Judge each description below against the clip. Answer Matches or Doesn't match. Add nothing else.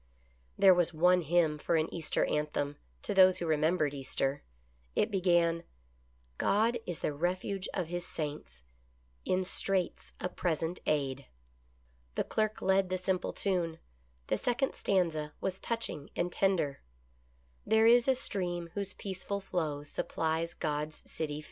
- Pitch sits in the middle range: Matches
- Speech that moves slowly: Doesn't match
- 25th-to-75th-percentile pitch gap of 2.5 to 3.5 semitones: Doesn't match